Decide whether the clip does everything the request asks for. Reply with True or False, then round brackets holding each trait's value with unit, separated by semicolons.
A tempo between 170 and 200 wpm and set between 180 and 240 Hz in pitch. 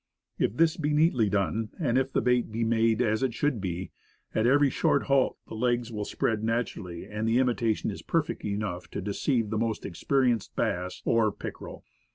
False (190 wpm; 115 Hz)